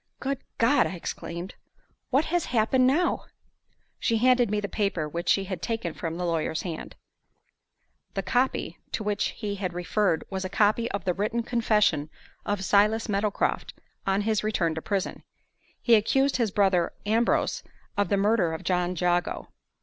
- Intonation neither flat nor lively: Yes, average, 4.2 semitones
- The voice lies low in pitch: No, high, 205 Hz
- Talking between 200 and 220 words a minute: No, average, 165 wpm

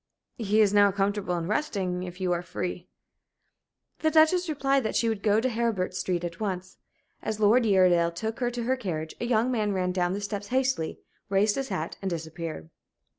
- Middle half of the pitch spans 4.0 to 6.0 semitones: Yes, average, 4.4 semitones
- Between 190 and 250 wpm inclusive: Yes, average, 200 wpm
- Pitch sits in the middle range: No, high, 200 Hz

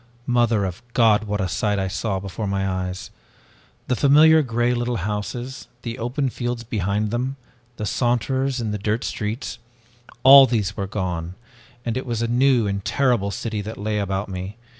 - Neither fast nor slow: Yes, average, 165 wpm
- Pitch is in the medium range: No, low, 110 Hz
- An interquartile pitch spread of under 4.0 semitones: Yes, average, 3.6 semitones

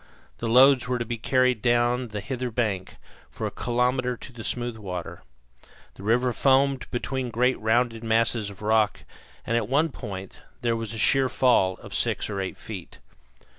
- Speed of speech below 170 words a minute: No, average, 175 wpm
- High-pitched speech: No, low, 120 Hz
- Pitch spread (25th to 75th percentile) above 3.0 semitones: No, narrow, 2.6 semitones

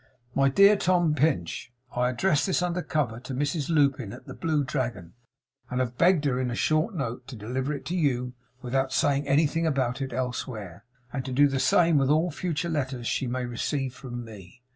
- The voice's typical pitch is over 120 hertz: Yes, low, 135 Hz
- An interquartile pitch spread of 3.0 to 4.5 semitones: Yes, average, 3.8 semitones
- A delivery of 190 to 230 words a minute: Yes, average, 200 wpm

